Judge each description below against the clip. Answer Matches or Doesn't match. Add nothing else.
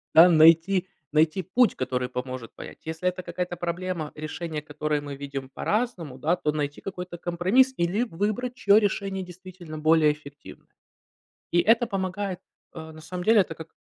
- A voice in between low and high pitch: Matches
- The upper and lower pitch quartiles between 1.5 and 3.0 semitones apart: Doesn't match